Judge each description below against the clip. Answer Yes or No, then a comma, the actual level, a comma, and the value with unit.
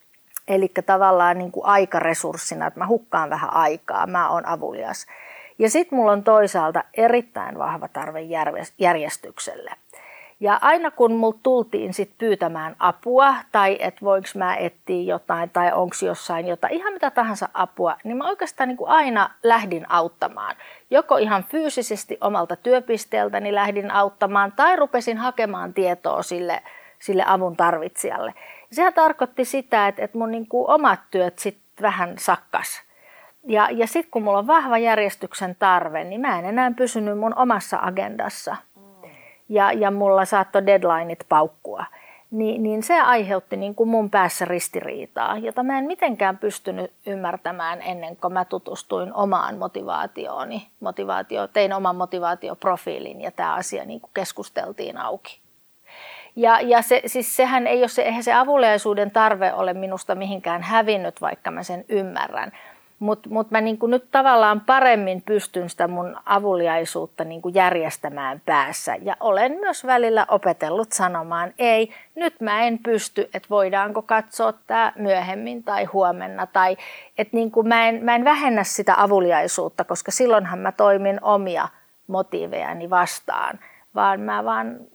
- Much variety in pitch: No, average, 4.3 semitones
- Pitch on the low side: No, high, 205 Hz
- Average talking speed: Yes, average, 140 wpm